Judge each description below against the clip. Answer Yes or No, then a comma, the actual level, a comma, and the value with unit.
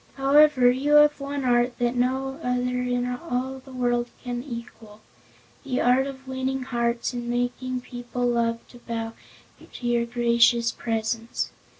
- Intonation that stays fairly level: Yes, narrow, 1.6 semitones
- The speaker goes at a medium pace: Yes, average, 150 wpm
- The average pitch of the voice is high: Yes, high, 245 Hz